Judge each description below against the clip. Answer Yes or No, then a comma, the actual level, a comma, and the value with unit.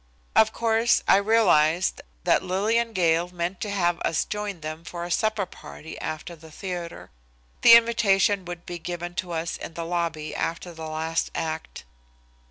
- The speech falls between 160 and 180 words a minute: Yes, average, 165 wpm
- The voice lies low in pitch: No, medium, 175 Hz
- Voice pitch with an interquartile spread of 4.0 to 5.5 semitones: No, average, 3.6 semitones